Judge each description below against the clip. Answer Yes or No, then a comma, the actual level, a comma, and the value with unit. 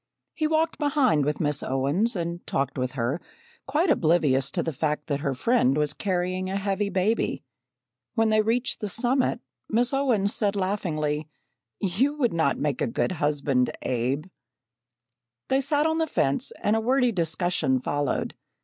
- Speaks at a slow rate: No, average, 160 wpm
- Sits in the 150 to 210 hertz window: Yes, medium, 185 Hz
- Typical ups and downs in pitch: No, wide, 8.2 semitones